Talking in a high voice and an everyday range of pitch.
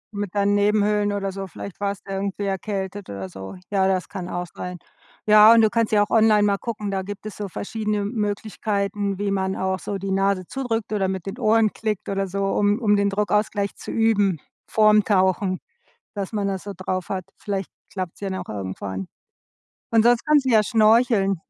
No: high, 200 Hz; narrow, 1.8 semitones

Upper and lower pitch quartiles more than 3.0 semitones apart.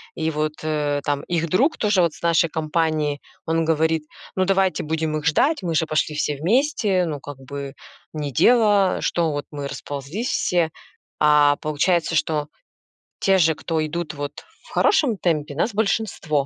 Yes: average, 3.7 semitones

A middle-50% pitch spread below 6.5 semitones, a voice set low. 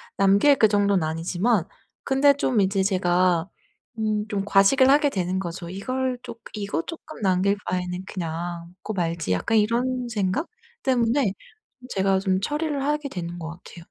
No: wide, 5.5 semitones; high, 200 Hz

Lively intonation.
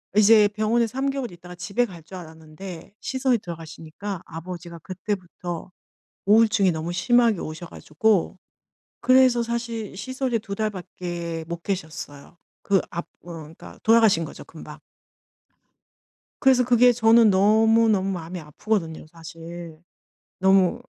No: average, 4.9 semitones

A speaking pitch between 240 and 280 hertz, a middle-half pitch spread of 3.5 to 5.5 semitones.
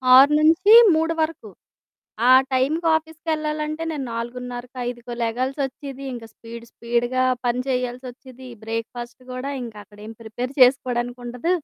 Yes: very high, 255 Hz; average, 4.0 semitones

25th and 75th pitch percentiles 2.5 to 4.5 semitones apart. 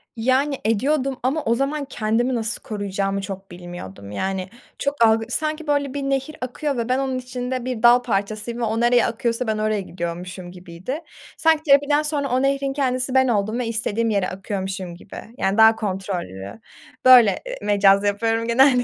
No: average, 5.0 semitones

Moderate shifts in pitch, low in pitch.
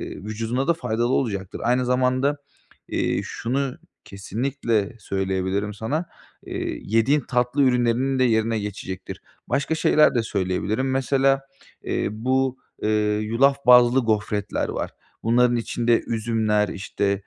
Yes: average, 3.7 semitones; low, 115 Hz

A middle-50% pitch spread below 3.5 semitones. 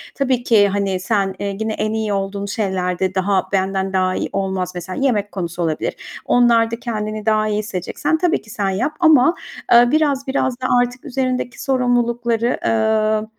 No: average, 4.1 semitones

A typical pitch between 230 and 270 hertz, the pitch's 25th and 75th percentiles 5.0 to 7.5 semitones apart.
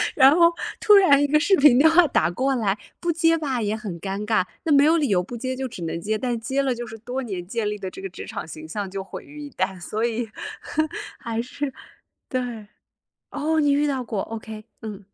Yes: high, 240 Hz; wide, 5.4 semitones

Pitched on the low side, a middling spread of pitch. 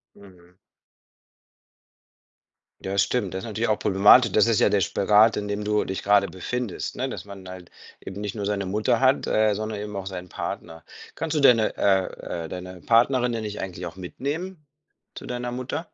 Yes: low, 105 Hz; average, 3.7 semitones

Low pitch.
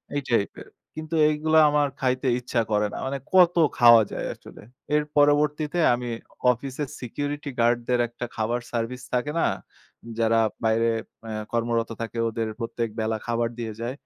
Yes: low, 120 Hz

